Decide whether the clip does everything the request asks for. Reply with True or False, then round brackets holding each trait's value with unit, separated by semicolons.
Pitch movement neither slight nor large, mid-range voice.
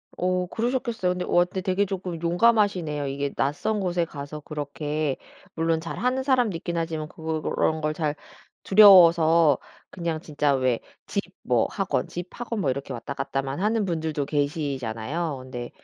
True (4.2 semitones; 165 Hz)